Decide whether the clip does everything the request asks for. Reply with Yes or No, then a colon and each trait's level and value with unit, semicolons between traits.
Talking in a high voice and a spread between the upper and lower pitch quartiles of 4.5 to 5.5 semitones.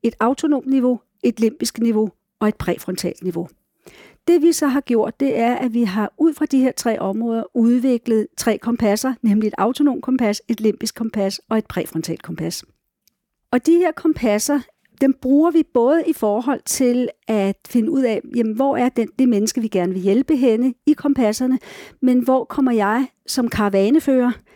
No: high, 235 Hz; average, 3.7 semitones